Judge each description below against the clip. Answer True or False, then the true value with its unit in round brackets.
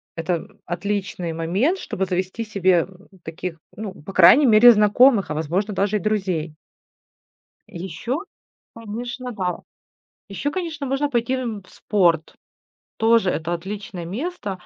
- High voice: True (200 Hz)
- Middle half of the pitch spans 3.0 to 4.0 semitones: False (4.8 semitones)